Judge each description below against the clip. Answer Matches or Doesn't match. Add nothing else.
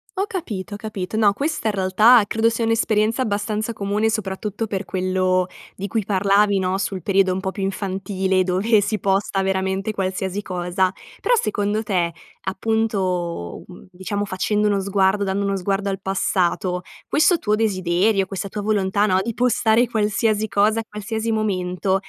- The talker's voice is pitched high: Matches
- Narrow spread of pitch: Matches